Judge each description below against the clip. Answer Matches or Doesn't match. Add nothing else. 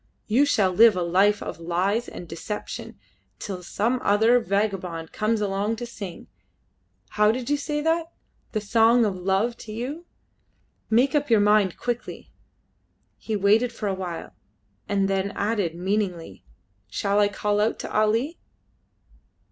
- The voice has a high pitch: Matches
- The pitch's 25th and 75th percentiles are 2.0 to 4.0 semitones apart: Matches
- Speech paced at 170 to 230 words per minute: Doesn't match